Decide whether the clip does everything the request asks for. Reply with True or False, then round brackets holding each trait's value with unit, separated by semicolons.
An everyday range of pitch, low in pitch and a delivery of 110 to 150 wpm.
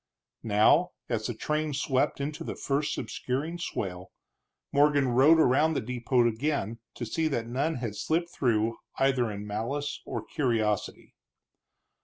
True (4.6 semitones; 130 Hz; 140 wpm)